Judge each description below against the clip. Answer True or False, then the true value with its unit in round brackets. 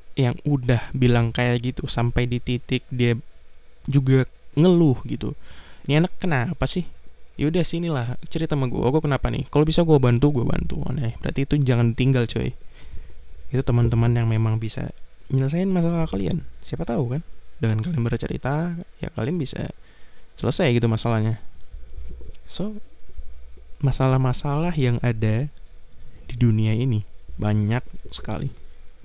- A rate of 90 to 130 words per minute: False (140 wpm)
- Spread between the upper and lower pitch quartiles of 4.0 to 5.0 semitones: True (4.7 semitones)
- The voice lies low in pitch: True (125 Hz)